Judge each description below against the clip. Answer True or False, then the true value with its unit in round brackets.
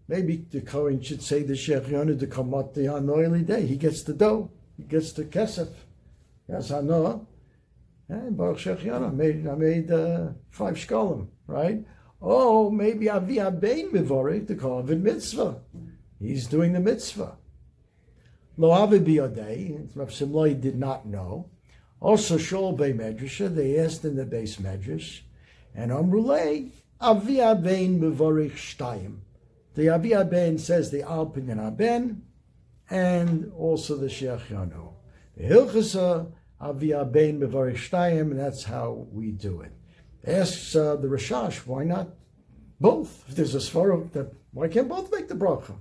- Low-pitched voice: False (155 Hz)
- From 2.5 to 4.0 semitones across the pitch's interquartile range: False (4.9 semitones)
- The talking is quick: False (145 wpm)